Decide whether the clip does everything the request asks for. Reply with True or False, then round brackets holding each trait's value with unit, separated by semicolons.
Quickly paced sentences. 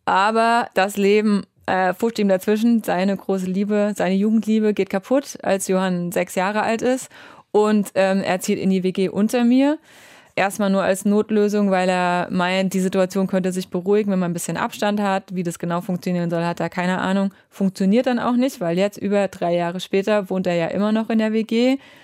True (200 wpm)